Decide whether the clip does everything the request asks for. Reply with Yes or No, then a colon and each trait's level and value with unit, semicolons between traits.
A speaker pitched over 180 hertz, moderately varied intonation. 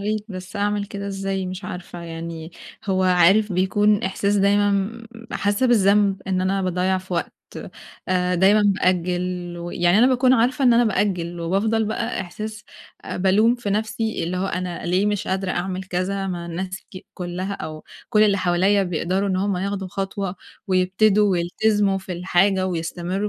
No: high, 190 Hz; narrow, 2.2 semitones